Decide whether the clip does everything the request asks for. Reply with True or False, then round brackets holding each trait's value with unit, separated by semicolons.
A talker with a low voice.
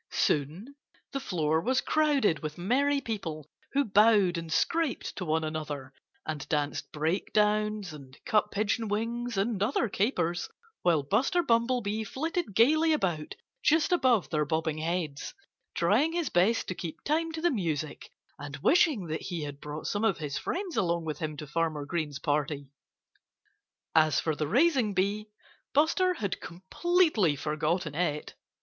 False (185 Hz)